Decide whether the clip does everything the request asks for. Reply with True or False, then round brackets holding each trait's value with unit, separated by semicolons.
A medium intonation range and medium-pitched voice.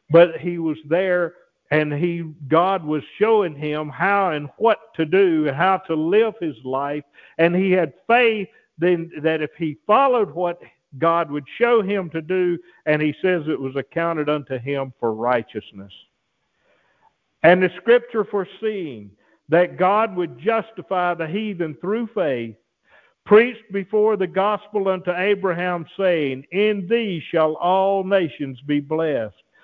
True (4.4 semitones; 175 Hz)